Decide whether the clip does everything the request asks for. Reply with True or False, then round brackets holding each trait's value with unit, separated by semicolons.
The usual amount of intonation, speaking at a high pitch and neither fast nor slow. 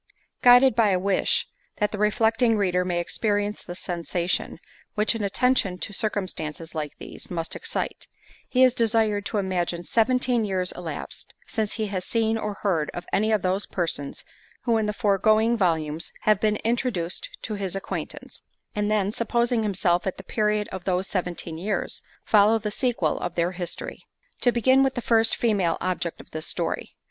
True (3.8 semitones; 205 Hz; 170 wpm)